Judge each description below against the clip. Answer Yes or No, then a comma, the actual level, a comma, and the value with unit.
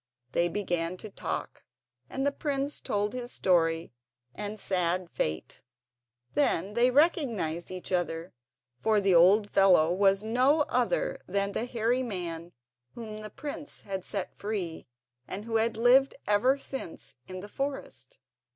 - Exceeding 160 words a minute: No, average, 140 wpm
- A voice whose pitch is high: Yes, high, 205 Hz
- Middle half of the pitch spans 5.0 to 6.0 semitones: Yes, average, 5.3 semitones